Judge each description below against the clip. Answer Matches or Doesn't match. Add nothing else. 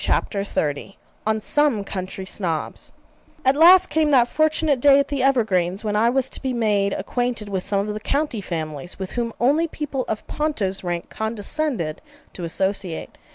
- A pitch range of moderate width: Doesn't match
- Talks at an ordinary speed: Matches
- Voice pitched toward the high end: Matches